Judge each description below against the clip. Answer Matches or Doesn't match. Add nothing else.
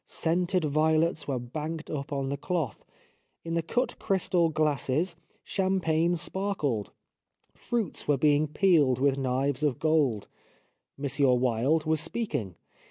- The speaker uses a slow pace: Matches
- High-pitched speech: Doesn't match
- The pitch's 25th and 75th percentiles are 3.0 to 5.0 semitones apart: Matches